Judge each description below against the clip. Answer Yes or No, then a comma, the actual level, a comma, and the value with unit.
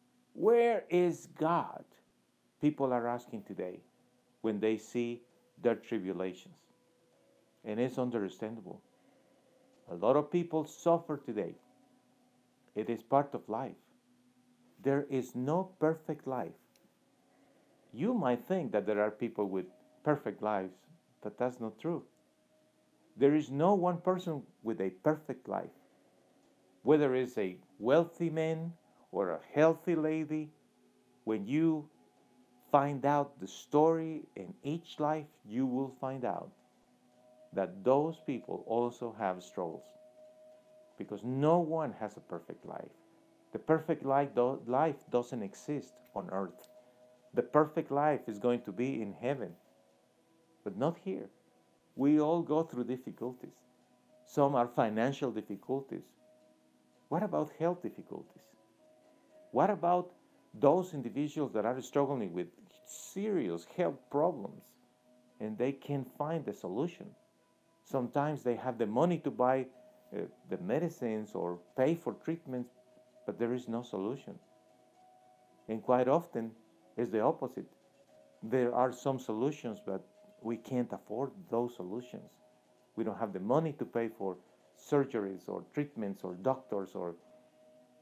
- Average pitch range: No, wide, 5.8 semitones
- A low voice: Yes, low, 125 Hz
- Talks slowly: Yes, slow, 130 wpm